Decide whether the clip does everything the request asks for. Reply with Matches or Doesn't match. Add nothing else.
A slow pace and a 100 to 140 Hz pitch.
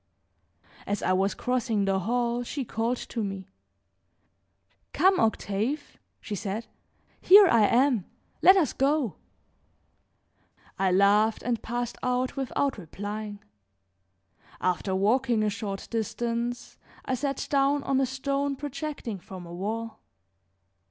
Doesn't match